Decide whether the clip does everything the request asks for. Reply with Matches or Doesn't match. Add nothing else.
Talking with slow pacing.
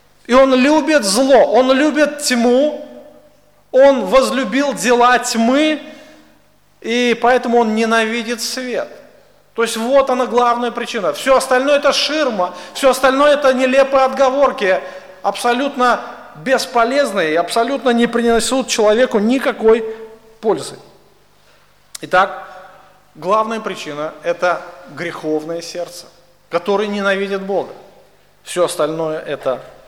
Matches